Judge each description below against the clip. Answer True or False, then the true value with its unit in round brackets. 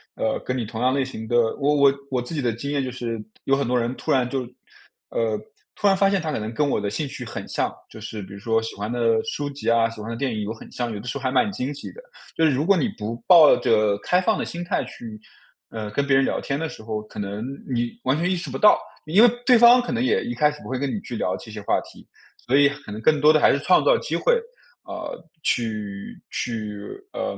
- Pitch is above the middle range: False (130 Hz)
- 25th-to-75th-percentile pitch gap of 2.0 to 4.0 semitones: False (5.0 semitones)